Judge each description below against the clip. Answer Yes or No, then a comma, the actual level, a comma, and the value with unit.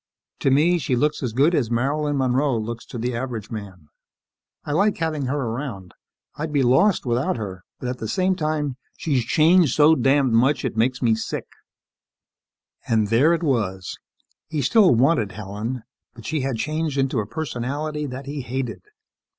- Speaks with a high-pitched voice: No, low, 130 Hz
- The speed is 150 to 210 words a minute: Yes, average, 175 wpm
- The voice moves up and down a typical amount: Yes, average, 4.5 semitones